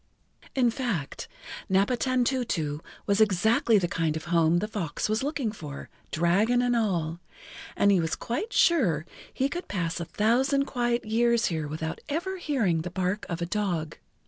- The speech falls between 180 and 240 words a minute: No, average, 165 wpm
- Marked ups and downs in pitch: Yes, wide, 6.5 semitones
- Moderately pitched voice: No, high, 210 Hz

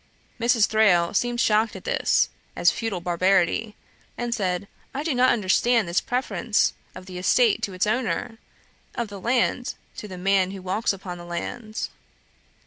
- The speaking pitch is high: Yes, high, 210 Hz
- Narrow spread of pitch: No, average, 4.3 semitones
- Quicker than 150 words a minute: Yes, average, 160 wpm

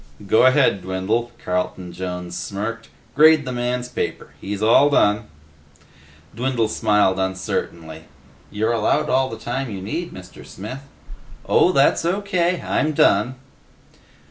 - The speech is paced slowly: Yes, slow, 125 wpm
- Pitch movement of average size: No, wide, 5.9 semitones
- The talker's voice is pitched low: Yes, low, 110 Hz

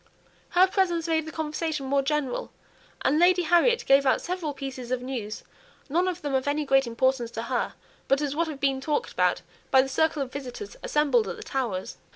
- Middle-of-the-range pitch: No, very high, 280 Hz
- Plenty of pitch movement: No, average, 3.5 semitones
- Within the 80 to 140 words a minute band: No, average, 200 wpm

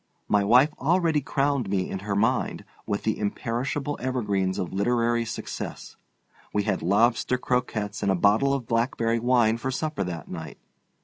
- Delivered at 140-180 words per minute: Yes, average, 160 wpm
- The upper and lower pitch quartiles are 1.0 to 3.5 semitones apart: No, average, 4.1 semitones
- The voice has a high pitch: No, low, 115 Hz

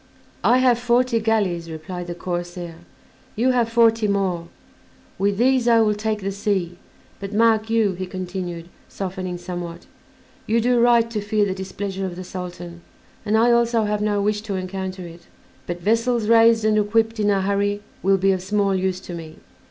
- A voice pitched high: Yes, high, 200 Hz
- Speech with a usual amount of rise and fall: Yes, average, 3.6 semitones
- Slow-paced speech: No, average, 180 wpm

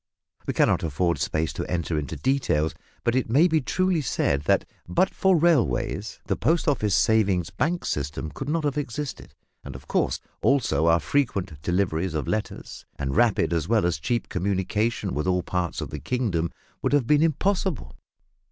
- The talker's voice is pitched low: Yes, low, 100 Hz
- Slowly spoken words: No, average, 175 wpm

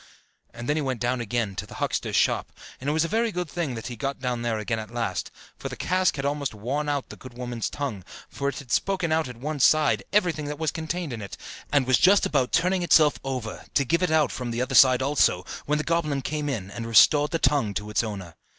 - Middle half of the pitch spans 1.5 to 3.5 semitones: No, average, 4.6 semitones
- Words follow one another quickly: Yes, fast, 250 wpm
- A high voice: No, medium, 140 Hz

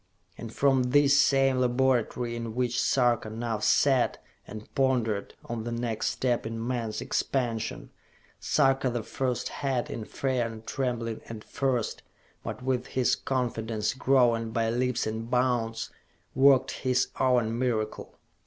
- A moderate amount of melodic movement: No, narrow, 2.3 semitones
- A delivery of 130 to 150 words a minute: Yes, slow, 135 wpm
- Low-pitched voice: Yes, low, 120 Hz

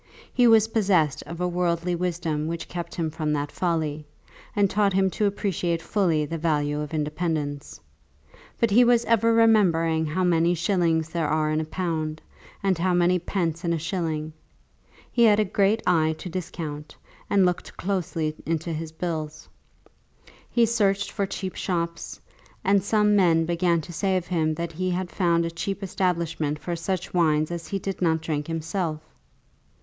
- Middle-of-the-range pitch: Yes, medium, 170 Hz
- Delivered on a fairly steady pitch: No, average, 3.1 semitones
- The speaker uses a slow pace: No, average, 175 wpm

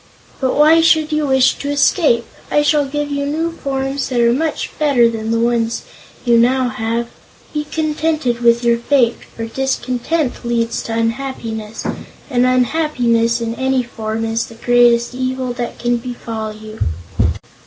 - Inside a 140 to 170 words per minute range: Yes, average, 155 wpm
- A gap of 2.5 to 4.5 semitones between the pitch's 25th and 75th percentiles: Yes, average, 3.4 semitones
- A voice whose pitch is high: Yes, high, 245 Hz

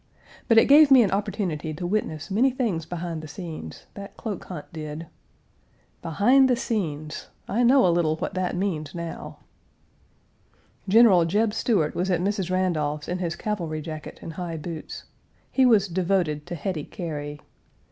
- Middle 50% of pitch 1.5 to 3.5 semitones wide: No, average, 4.7 semitones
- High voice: No, medium, 180 Hz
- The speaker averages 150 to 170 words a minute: Yes, average, 160 wpm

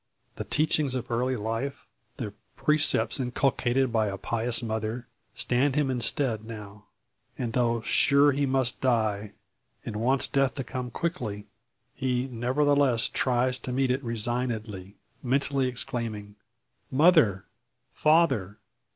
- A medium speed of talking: No, slow, 125 wpm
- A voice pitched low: Yes, low, 125 Hz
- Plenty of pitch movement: No, average, 3.3 semitones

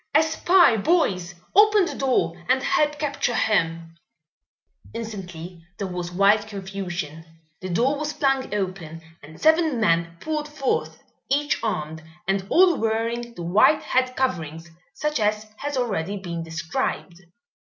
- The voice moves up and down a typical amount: No, wide, 8.1 semitones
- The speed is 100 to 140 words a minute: Yes, slow, 135 wpm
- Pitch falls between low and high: No, high, 210 Hz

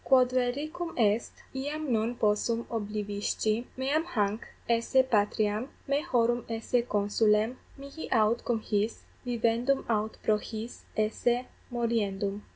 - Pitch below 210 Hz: No, high, 230 Hz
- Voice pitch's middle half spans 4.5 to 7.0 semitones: No, average, 2.9 semitones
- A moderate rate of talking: No, slow, 120 wpm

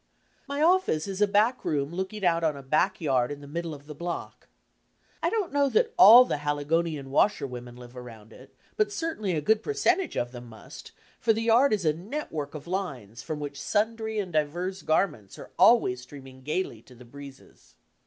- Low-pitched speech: No, medium, 160 Hz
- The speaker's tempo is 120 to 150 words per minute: No, average, 195 wpm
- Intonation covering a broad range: Yes, wide, 7.4 semitones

